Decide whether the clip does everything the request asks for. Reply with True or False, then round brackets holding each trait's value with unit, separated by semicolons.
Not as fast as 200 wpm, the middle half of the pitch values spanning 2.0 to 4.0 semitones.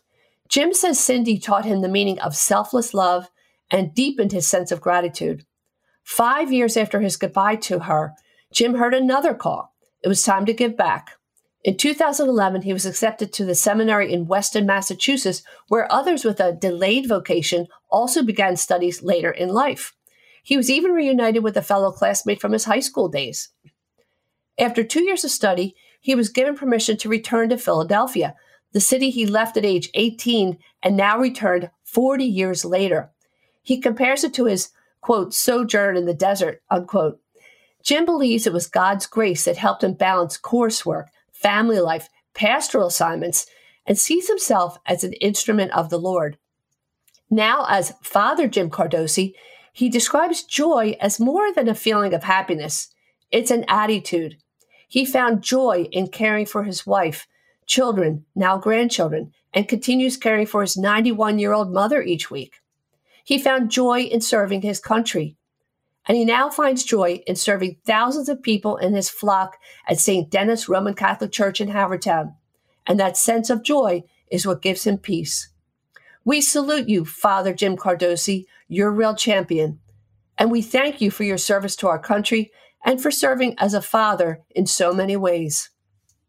False (165 wpm; 4.8 semitones)